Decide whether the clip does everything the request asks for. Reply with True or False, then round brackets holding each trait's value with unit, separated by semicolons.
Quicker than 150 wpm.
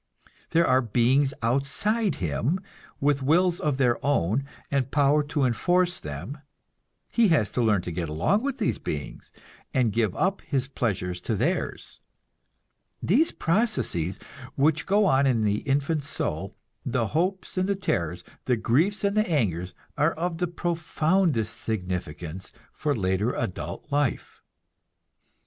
False (145 wpm)